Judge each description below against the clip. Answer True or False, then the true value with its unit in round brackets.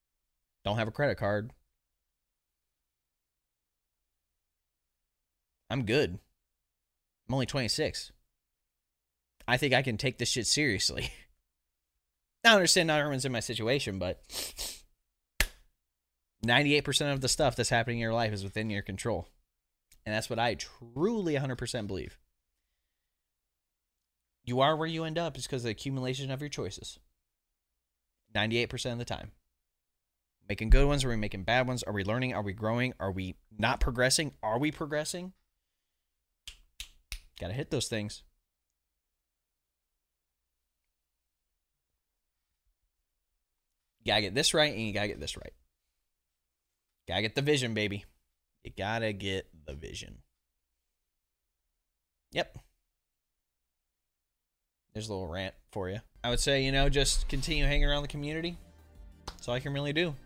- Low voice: True (75 Hz)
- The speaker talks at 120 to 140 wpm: True (135 wpm)